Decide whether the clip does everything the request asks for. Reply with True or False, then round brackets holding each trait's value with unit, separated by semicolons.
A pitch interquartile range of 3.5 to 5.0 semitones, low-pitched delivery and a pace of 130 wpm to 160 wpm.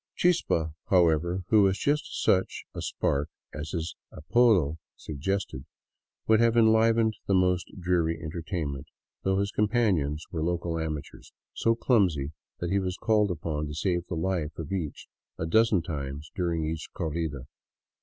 True (4.2 semitones; 85 Hz; 155 wpm)